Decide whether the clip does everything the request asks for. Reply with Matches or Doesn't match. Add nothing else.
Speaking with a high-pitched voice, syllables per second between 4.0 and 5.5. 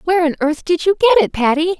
Doesn't match